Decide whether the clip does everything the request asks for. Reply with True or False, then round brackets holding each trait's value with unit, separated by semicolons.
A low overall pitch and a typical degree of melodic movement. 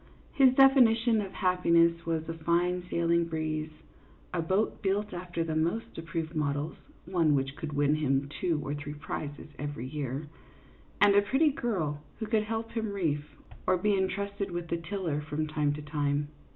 False (165 Hz; 5.0 semitones)